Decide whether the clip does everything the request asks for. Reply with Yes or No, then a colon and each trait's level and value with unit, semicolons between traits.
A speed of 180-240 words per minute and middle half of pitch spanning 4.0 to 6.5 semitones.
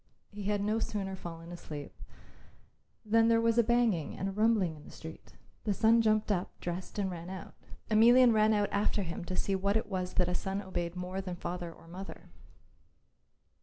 No: average, 195 wpm; average, 3.3 semitones